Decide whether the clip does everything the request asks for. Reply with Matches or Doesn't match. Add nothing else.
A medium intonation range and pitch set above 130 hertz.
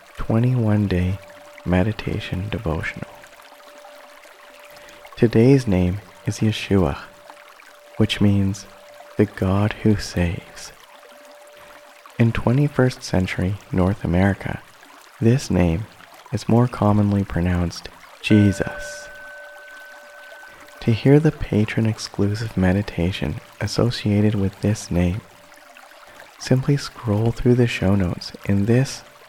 Doesn't match